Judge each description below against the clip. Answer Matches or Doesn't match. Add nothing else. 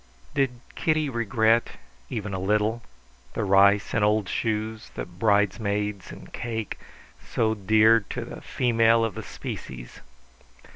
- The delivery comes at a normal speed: Doesn't match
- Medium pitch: Doesn't match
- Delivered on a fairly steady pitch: Matches